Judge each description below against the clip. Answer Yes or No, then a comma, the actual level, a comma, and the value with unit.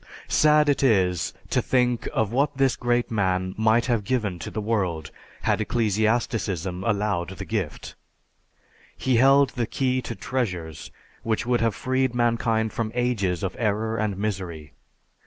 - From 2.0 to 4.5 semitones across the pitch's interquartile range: Yes, average, 4.1 semitones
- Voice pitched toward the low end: Yes, low, 110 Hz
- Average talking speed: Yes, average, 150 wpm